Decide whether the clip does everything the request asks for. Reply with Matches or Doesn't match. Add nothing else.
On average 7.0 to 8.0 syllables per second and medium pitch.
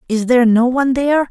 Doesn't match